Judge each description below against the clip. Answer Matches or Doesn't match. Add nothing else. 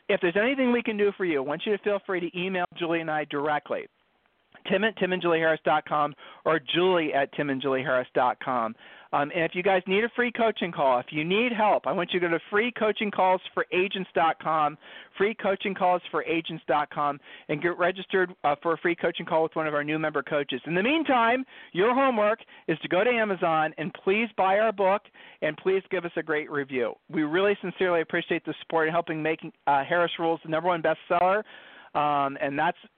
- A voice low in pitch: Doesn't match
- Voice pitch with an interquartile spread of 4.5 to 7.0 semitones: Doesn't match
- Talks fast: Matches